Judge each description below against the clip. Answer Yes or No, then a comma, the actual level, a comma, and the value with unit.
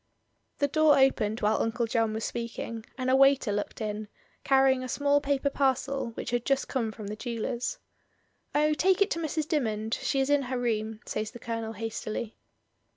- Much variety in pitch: No, average, 3.9 semitones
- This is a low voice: No, high, 245 Hz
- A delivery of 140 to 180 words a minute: No, average, 190 wpm